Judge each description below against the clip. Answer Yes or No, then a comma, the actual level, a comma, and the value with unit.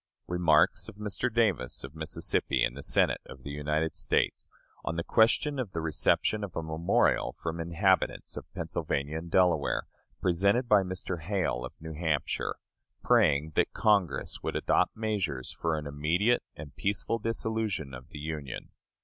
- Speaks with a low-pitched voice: Yes, very low, 85 Hz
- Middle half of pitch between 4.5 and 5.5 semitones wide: Yes, average, 5.1 semitones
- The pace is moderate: Yes, average, 160 wpm